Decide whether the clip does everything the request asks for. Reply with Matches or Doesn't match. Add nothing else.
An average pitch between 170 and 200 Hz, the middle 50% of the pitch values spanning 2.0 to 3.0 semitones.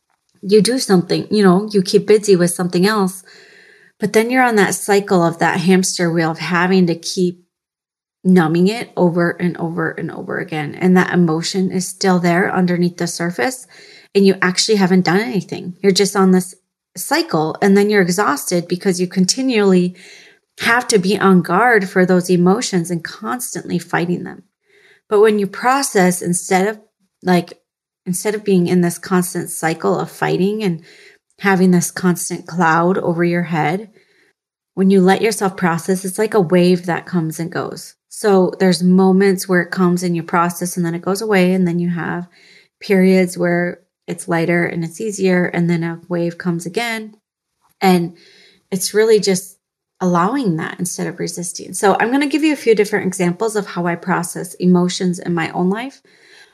Matches